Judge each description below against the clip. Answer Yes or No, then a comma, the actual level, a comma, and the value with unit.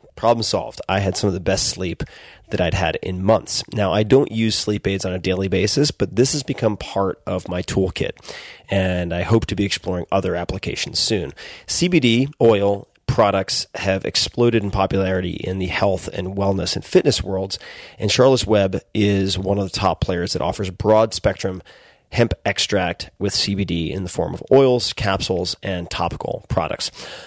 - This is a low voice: Yes, low, 100 Hz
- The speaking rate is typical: Yes, average, 180 wpm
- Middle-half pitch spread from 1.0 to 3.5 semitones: Yes, average, 2.8 semitones